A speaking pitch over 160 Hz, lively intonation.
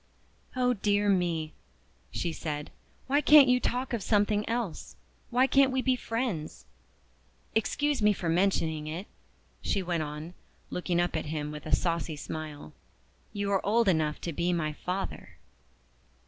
Yes: medium, 185 Hz; wide, 6.6 semitones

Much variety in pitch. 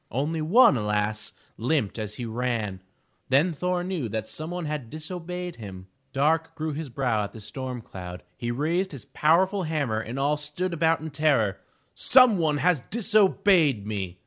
Yes: wide, 7.0 semitones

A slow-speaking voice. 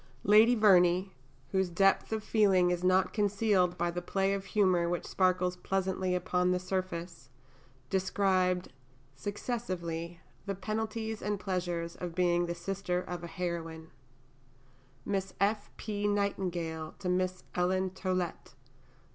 Yes: slow, 130 wpm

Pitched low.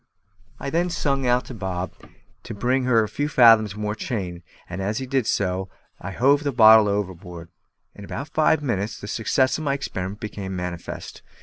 Yes: low, 110 Hz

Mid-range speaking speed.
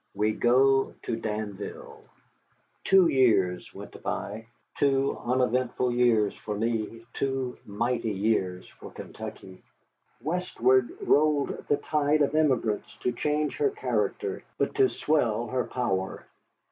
No: slow, 120 wpm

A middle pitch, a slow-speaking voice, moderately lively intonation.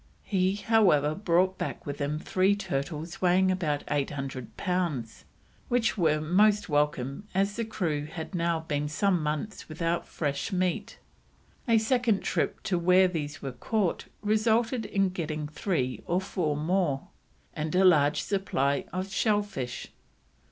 No: medium, 175 Hz; average, 145 wpm; average, 4.9 semitones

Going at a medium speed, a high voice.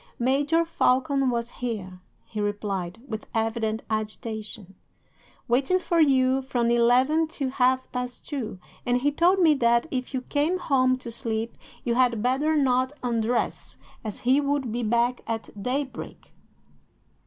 Yes: average, 145 wpm; very high, 250 Hz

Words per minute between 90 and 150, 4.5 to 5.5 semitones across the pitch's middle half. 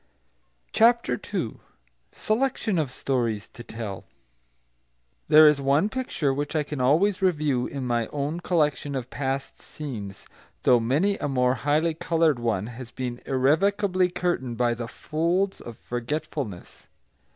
Yes: slow, 135 wpm; average, 5.2 semitones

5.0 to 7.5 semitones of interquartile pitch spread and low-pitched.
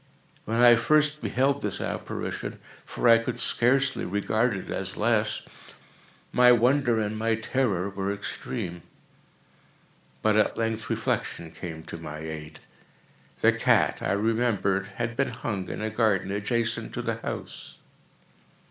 No: average, 3.4 semitones; low, 110 Hz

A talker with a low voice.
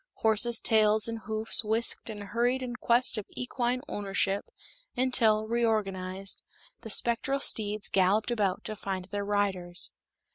No: high, 215 Hz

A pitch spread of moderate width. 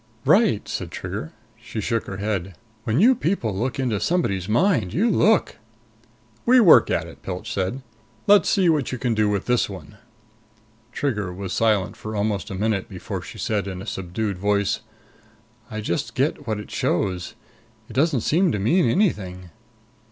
No: wide, 6.3 semitones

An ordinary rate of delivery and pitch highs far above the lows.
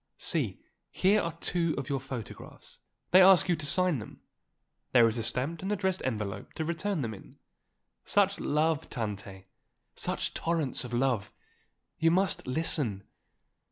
Yes: average, 150 wpm; wide, 6.7 semitones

